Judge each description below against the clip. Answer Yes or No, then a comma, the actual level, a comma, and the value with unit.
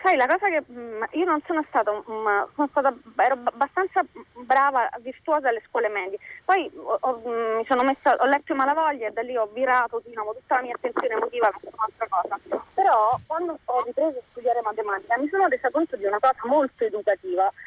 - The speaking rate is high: Yes, fast, 195 wpm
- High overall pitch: Yes, very high, 260 Hz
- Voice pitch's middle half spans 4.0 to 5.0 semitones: No, wide, 5.5 semitones